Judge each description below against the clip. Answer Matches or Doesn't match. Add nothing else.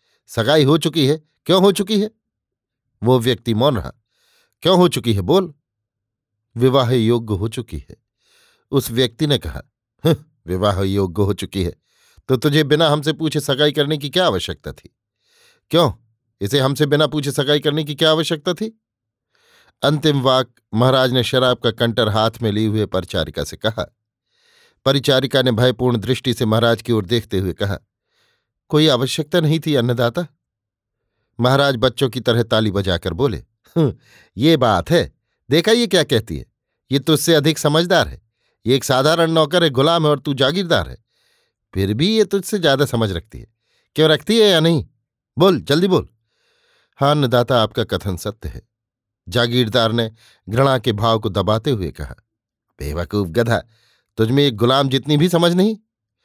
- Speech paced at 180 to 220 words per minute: Doesn't match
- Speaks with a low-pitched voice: Matches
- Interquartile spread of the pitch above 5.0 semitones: Matches